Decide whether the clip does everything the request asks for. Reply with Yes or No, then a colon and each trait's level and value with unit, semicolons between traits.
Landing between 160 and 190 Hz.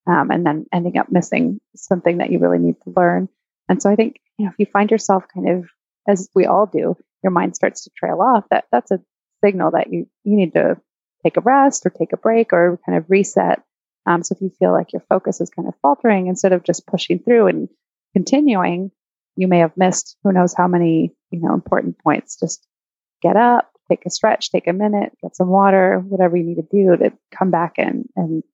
Yes: medium, 185 Hz